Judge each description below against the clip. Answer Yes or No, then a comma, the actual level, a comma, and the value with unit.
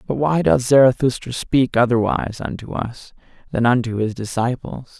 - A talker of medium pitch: No, low, 120 Hz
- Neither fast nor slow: Yes, average, 145 wpm